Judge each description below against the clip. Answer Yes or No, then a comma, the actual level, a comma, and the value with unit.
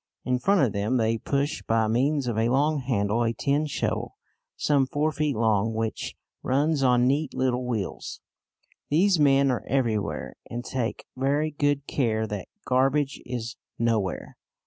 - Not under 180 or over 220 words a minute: No, average, 155 wpm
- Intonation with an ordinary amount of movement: Yes, average, 4.0 semitones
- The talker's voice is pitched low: Yes, low, 130 Hz